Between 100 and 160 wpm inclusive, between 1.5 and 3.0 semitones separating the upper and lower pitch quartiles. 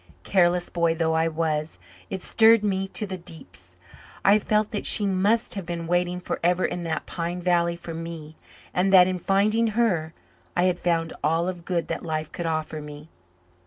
No: average, 185 wpm; average, 2.7 semitones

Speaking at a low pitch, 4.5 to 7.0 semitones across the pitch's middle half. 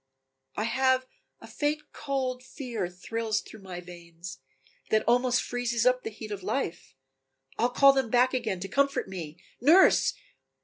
No: high, 235 Hz; average, 5.1 semitones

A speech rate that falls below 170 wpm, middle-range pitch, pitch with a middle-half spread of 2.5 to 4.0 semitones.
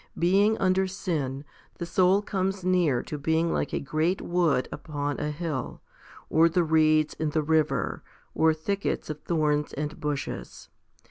Yes: average, 150 wpm; medium, 160 Hz; average, 3.2 semitones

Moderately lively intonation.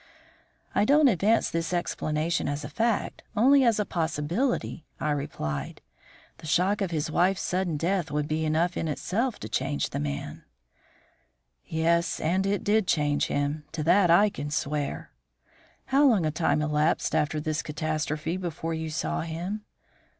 Yes: average, 4.3 semitones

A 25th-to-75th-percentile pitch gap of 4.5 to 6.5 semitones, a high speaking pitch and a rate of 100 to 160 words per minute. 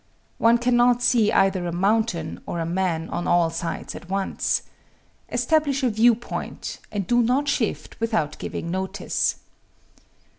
Yes: wide, 5.6 semitones; high, 205 Hz; average, 145 wpm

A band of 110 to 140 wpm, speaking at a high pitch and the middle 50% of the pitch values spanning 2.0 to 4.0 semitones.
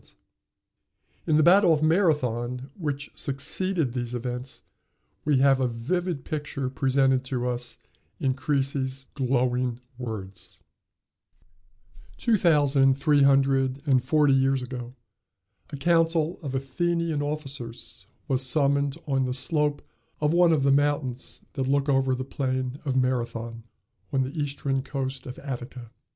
No: slow, 135 wpm; low, 135 Hz; narrow, 2.4 semitones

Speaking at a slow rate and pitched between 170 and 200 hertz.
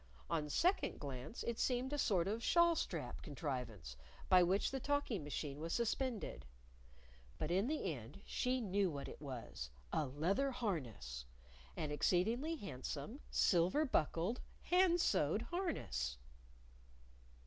Yes: slow, 130 wpm; medium, 185 Hz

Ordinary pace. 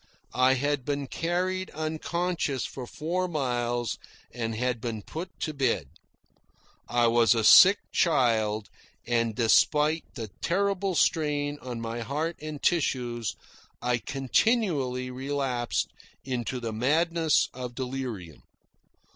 No: slow, 115 wpm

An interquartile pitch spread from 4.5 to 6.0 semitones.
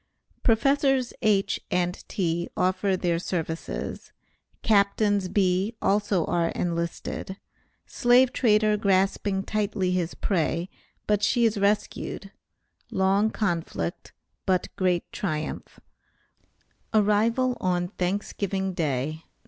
No: average, 3.0 semitones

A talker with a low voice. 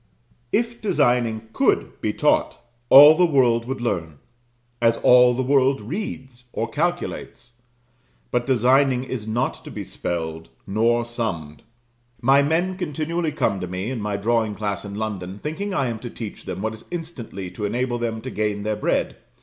Yes: low, 120 Hz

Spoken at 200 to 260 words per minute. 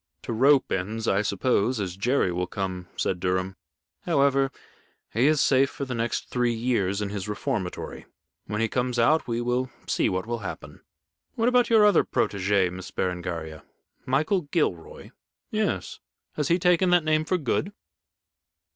No: average, 160 wpm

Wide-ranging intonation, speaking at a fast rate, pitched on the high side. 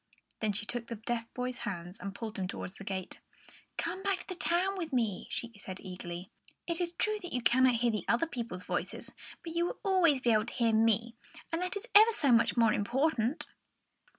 Yes: wide, 7.8 semitones; fast, 215 wpm; high, 240 Hz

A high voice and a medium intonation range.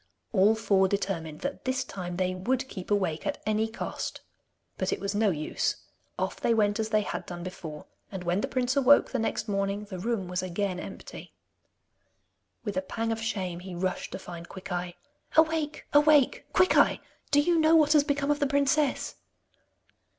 No: high, 210 Hz; wide, 6.4 semitones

